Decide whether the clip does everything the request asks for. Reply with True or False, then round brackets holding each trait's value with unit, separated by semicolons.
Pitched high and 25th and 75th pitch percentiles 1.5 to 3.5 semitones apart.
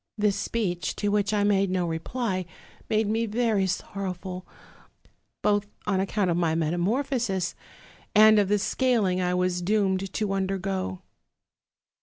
True (195 Hz; 2.6 semitones)